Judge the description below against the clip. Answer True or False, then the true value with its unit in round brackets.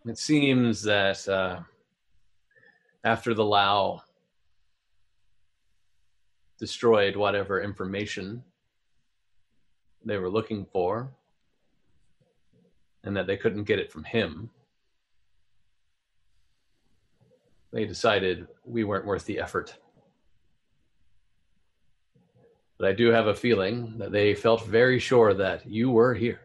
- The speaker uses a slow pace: True (100 wpm)